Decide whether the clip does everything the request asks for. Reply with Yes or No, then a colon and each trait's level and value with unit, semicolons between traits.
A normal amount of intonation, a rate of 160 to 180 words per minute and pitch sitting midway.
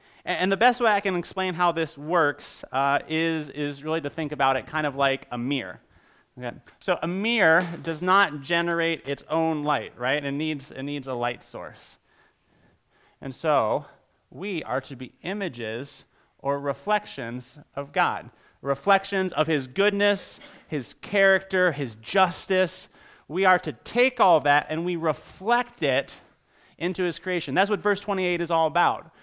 Yes: average, 4.9 semitones; average, 165 wpm; medium, 160 Hz